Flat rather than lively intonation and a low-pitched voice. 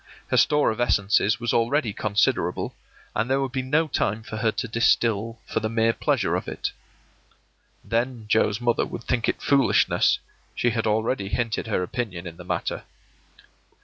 Yes: narrow, 2.2 semitones; low, 115 Hz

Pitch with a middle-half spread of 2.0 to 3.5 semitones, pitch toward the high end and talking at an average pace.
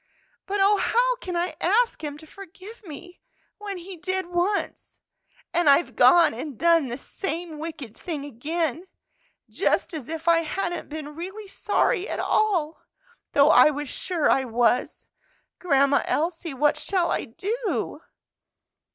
No: average, 4.2 semitones; very high, 335 Hz; average, 145 wpm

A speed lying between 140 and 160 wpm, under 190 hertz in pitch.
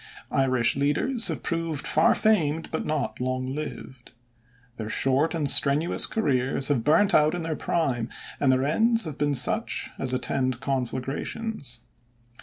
Yes: average, 145 wpm; medium, 140 Hz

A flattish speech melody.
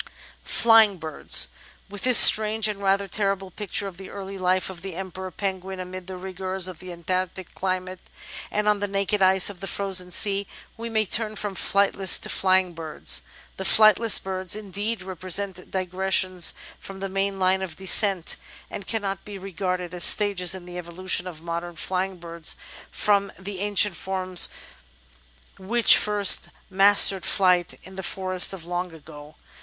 Yes: narrow, 1.6 semitones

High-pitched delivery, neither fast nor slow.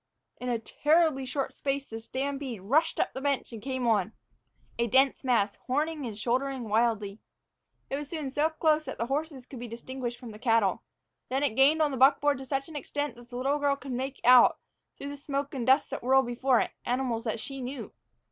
No: very high, 265 Hz; fast, 215 wpm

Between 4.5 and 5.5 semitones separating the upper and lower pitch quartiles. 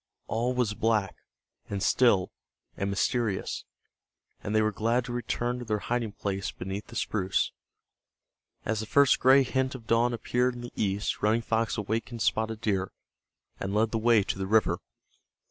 No: average, 2.8 semitones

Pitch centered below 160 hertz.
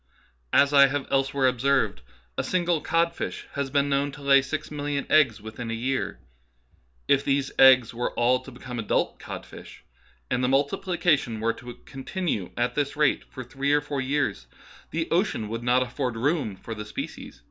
Yes: low, 135 Hz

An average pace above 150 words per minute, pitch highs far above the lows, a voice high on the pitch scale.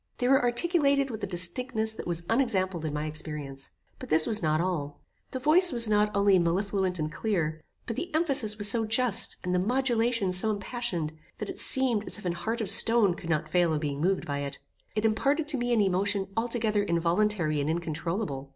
Yes: fast, 205 wpm; wide, 5.8 semitones; high, 200 Hz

